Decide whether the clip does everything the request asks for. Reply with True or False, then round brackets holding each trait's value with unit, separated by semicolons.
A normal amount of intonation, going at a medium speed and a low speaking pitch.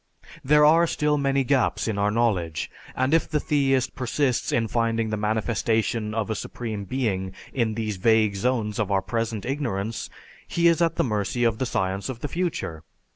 True (4.2 semitones; 180 wpm; 115 Hz)